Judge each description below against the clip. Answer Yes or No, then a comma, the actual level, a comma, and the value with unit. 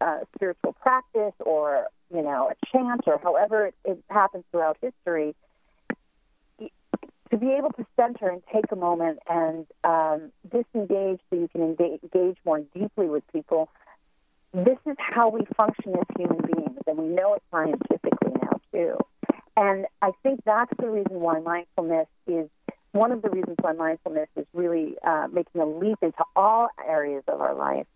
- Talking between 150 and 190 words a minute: Yes, average, 165 wpm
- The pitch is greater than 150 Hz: Yes, medium, 185 Hz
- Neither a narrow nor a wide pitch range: No, wide, 5.7 semitones